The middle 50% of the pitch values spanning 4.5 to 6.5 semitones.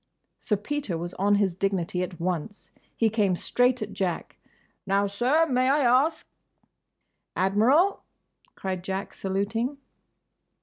Yes: average, 4.8 semitones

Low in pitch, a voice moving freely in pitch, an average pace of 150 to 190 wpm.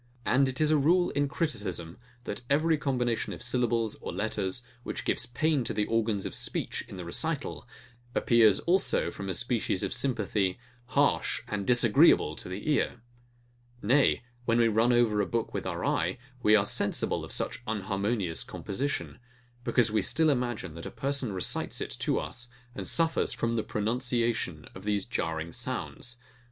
No: low, 115 Hz; average, 4.3 semitones; average, 170 wpm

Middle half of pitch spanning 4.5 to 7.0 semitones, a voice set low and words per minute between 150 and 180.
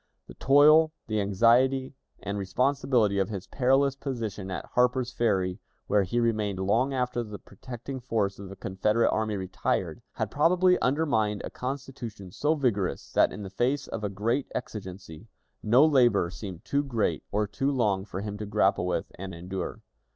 Yes: average, 4.9 semitones; low, 110 Hz; average, 165 wpm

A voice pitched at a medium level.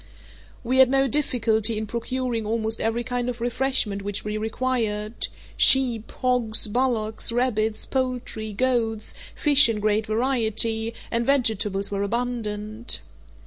No: high, 230 Hz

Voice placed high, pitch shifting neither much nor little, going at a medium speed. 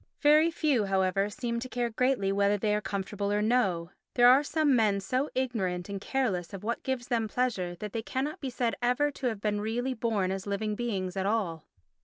No: high, 220 Hz; average, 4.2 semitones; fast, 210 wpm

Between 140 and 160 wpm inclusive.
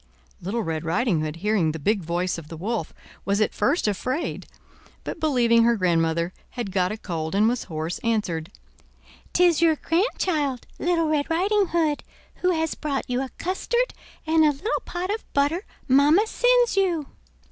No: average, 170 wpm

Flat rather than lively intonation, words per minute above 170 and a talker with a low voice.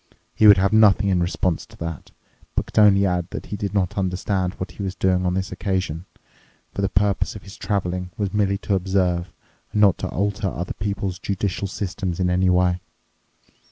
Yes: narrow, 1.8 semitones; average, 195 wpm; very low, 95 Hz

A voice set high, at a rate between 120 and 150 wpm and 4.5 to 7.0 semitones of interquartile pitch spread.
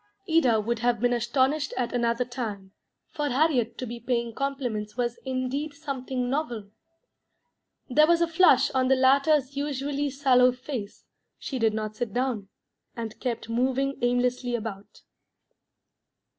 No: very high, 250 Hz; average, 140 wpm; average, 2.8 semitones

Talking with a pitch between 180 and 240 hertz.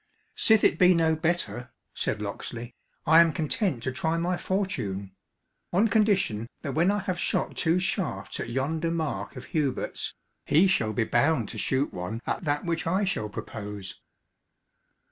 No: medium, 160 Hz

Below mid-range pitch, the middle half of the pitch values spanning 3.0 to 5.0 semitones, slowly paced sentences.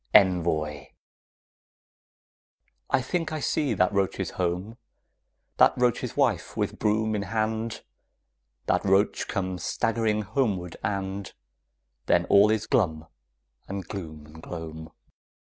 Yes: low, 100 Hz; average, 3.9 semitones; slow, 110 wpm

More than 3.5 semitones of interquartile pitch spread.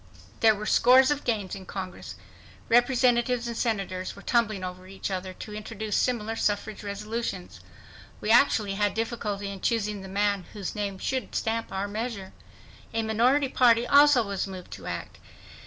No: average, 3.2 semitones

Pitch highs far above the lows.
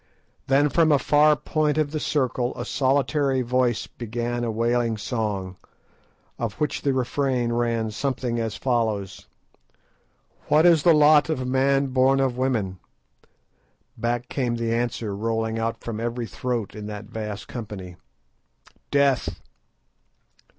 No: average, 3.2 semitones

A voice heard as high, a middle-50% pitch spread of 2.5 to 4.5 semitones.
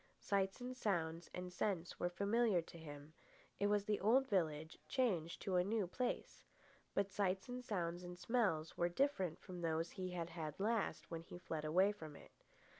No: medium, 180 Hz; average, 3.9 semitones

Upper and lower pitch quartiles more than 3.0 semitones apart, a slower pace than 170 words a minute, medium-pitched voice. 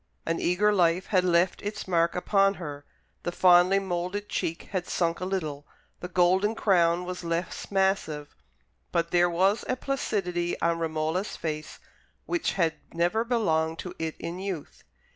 No: narrow, 2.6 semitones; average, 155 wpm; medium, 175 Hz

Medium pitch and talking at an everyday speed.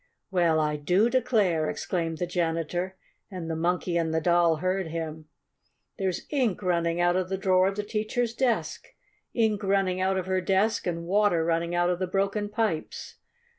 Yes: medium, 180 Hz; average, 175 wpm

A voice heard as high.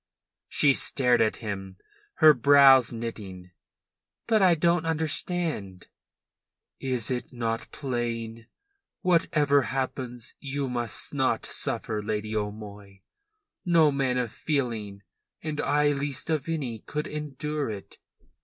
No: low, 130 Hz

